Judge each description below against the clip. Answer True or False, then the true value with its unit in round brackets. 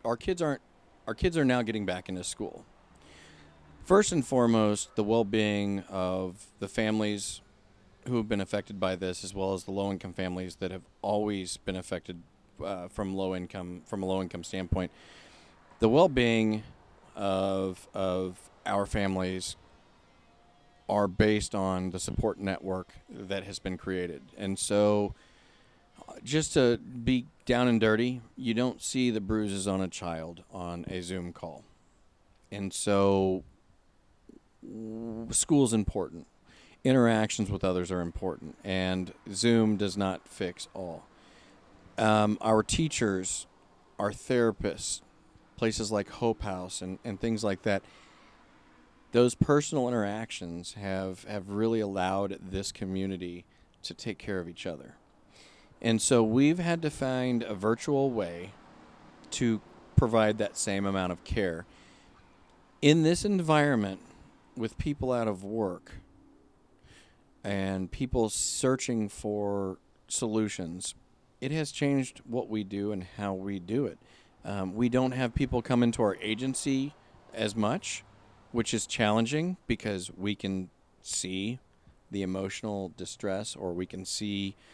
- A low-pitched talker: True (100 Hz)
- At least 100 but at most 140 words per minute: True (135 wpm)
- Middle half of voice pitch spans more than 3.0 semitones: True (3.5 semitones)